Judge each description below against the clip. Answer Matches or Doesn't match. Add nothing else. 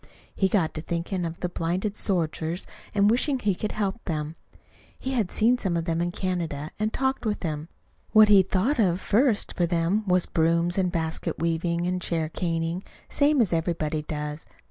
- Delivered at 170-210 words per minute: Matches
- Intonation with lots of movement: Doesn't match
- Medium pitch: Matches